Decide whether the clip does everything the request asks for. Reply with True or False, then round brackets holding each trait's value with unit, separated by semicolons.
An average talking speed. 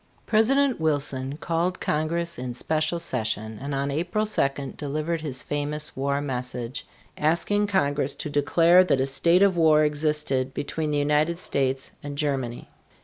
True (145 wpm)